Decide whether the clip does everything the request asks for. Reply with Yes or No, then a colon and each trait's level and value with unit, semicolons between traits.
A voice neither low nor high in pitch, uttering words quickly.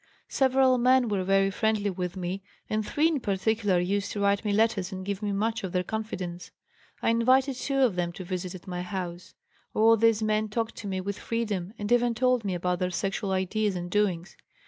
No: high, 205 Hz; fast, 210 wpm